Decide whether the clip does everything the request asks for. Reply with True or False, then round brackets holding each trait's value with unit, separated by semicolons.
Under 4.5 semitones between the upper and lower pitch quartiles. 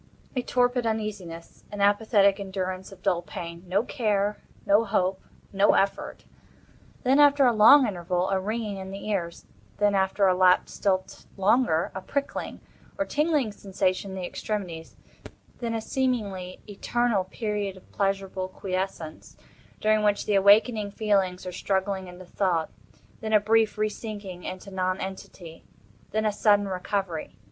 True (2.5 semitones)